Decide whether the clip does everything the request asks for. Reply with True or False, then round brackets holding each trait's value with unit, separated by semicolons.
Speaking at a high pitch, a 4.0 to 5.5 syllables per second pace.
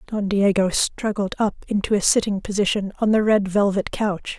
True (200 Hz; 5.0 syllables/s)